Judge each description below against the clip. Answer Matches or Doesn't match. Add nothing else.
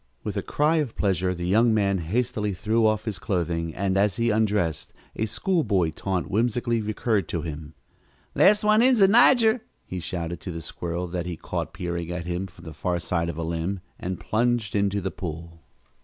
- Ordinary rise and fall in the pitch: Matches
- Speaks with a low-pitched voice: Matches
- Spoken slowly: Doesn't match